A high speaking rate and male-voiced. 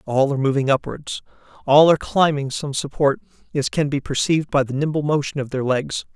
No: average, 195 wpm; male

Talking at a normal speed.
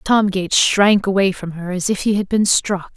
No: fast, 245 wpm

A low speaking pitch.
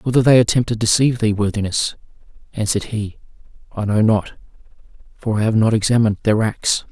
Yes: low, 110 Hz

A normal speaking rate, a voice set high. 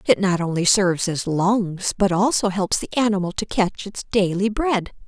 Yes: average, 190 wpm; high, 195 Hz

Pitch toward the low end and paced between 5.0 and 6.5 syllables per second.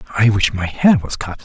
Yes: low, 110 Hz; 5.9 syllables/s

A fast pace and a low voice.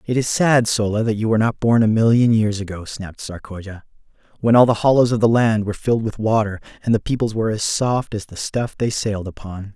Yes: fast, 235 wpm; low, 110 Hz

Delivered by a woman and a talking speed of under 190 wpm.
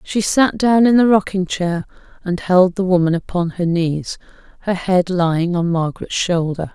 Yes: female; average, 180 wpm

